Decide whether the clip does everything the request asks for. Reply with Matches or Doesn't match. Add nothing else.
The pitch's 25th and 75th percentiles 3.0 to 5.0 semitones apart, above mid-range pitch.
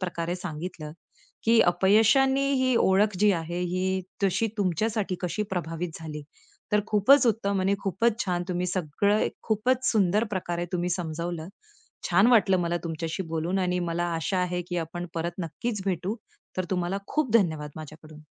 Doesn't match